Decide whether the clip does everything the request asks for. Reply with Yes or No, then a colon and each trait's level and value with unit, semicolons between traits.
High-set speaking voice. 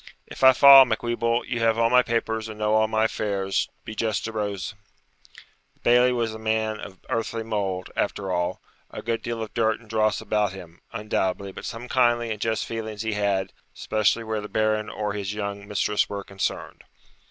No: low, 110 Hz